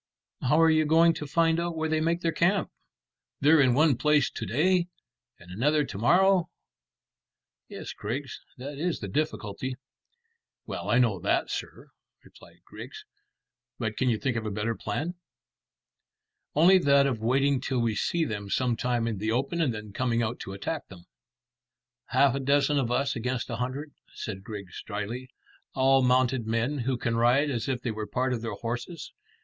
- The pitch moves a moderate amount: Yes, average, 4.7 semitones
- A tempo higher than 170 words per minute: Yes, average, 180 wpm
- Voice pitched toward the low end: Yes, low, 130 Hz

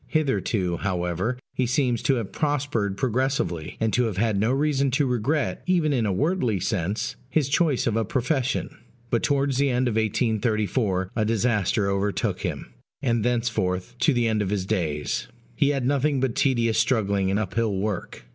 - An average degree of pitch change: Yes, average, 4.7 semitones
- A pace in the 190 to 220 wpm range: No, average, 175 wpm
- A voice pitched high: No, low, 115 Hz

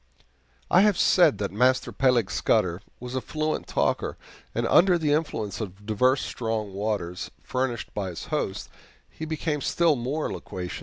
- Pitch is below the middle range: Yes, low, 125 Hz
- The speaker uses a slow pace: No, average, 155 wpm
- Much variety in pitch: Yes, wide, 6.9 semitones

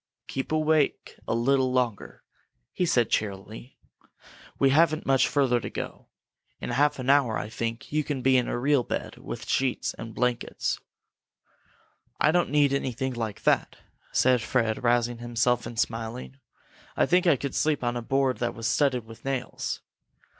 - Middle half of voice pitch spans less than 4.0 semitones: Yes, average, 2.9 semitones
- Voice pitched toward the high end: No, low, 125 Hz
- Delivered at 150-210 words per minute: Yes, average, 170 wpm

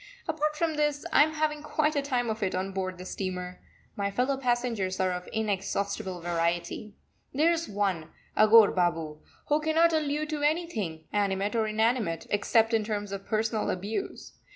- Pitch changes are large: Yes, wide, 7.6 semitones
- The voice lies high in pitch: Yes, high, 215 Hz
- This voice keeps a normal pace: Yes, average, 170 wpm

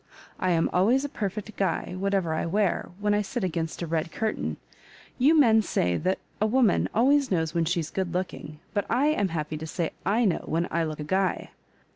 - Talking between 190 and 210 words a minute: Yes, average, 200 wpm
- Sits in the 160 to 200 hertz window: Yes, high, 190 Hz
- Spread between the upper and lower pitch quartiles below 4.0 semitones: No, average, 4.8 semitones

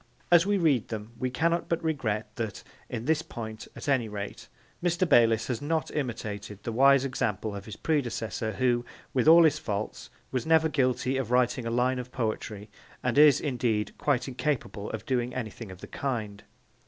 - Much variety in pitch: No, average, 4.5 semitones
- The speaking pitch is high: No, low, 125 Hz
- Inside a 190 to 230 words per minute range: No, average, 180 wpm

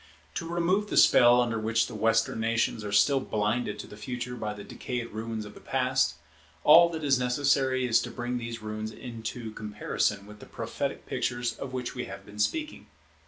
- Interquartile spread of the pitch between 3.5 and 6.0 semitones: No, average, 3.1 semitones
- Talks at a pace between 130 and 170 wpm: No, average, 195 wpm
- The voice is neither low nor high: No, low, 115 Hz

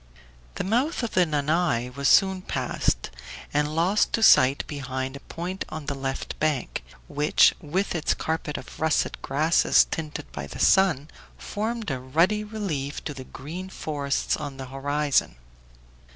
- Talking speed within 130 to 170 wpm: Yes, average, 150 wpm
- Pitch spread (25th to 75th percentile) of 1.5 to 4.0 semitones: No, average, 5.1 semitones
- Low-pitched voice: No, medium, 150 Hz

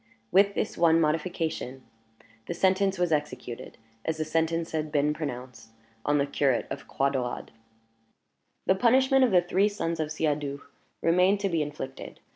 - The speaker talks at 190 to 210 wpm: No, average, 155 wpm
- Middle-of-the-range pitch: Yes, medium, 160 Hz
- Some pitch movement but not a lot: Yes, average, 4.1 semitones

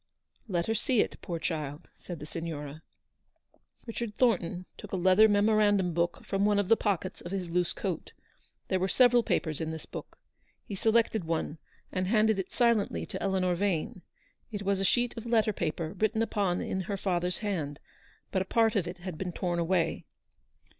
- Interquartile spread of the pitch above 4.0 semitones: No, average, 3.6 semitones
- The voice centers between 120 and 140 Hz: No, high, 190 Hz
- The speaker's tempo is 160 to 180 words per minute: No, average, 190 wpm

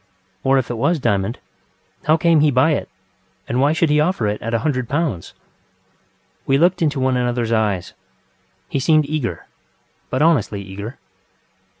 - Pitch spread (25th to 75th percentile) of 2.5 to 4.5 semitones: No, average, 5.1 semitones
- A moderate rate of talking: Yes, average, 170 wpm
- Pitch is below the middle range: Yes, low, 130 Hz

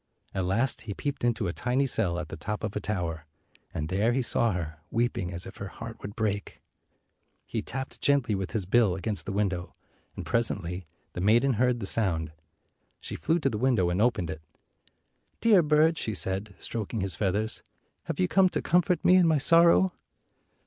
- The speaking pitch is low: Yes, low, 105 Hz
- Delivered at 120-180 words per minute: No, average, 190 wpm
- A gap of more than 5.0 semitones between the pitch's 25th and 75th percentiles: Yes, wide, 5.4 semitones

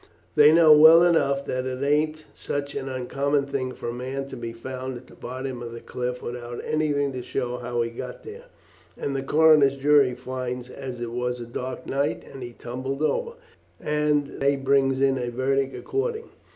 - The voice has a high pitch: No, low, 135 Hz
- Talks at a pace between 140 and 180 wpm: No, average, 190 wpm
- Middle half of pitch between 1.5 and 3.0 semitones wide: Yes, narrow, 2.5 semitones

